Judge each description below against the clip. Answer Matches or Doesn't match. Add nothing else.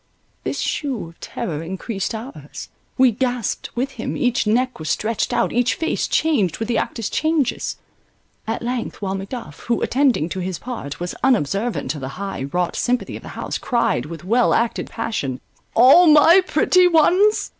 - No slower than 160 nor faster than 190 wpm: Matches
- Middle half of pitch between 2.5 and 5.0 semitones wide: Doesn't match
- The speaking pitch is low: Doesn't match